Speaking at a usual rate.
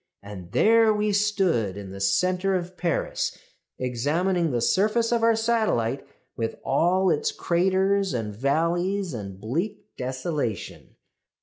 No: slow, 125 wpm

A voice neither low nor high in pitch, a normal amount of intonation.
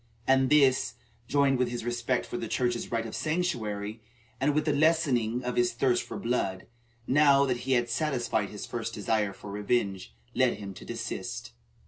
No: low, 120 Hz; average, 3.5 semitones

